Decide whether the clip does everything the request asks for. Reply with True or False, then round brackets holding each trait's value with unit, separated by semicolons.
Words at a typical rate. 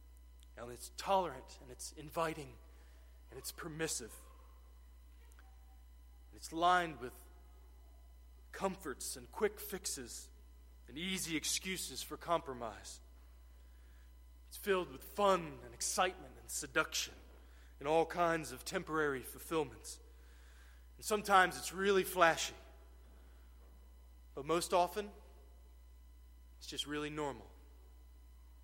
False (100 wpm)